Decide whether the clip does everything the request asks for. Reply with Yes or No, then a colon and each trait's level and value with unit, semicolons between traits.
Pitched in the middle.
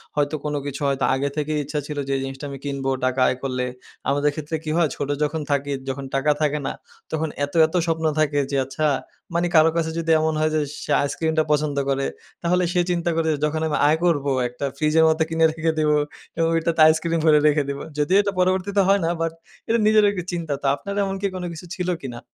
Yes: medium, 155 Hz